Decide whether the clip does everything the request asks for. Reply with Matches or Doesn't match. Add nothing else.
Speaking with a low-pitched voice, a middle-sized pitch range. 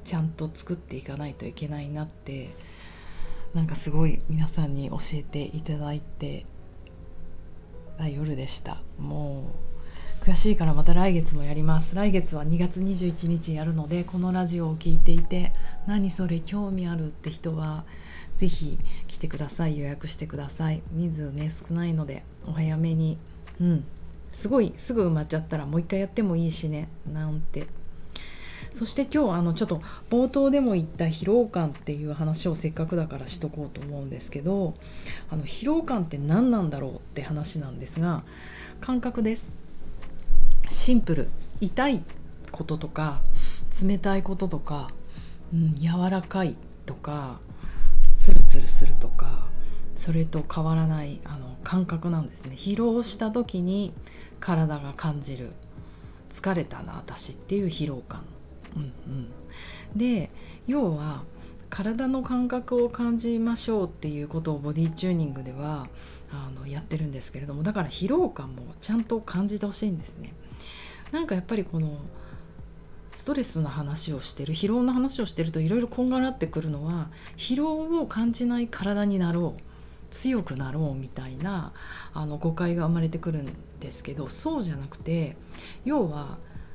Doesn't match